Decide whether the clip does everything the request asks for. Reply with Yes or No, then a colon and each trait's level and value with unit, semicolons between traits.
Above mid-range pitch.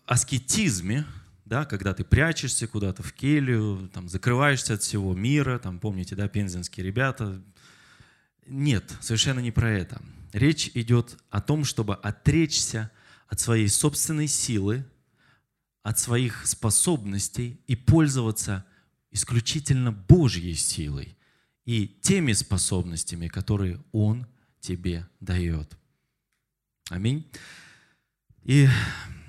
No: low, 115 Hz